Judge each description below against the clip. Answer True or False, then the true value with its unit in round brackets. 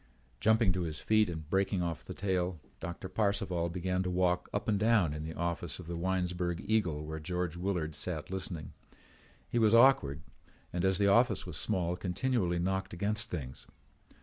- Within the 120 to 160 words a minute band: False (175 wpm)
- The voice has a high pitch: False (90 Hz)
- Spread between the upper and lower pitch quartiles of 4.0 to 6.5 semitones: False (2.7 semitones)